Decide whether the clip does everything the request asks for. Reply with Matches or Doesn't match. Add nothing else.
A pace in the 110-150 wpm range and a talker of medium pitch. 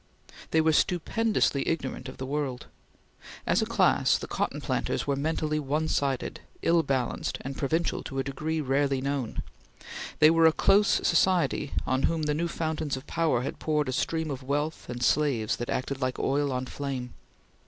Doesn't match